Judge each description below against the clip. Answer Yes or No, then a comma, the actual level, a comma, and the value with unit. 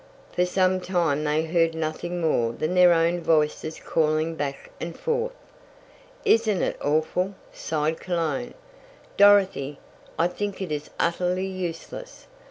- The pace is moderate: No, slow, 130 wpm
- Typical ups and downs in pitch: Yes, average, 3.0 semitones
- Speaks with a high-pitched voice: No, medium, 170 Hz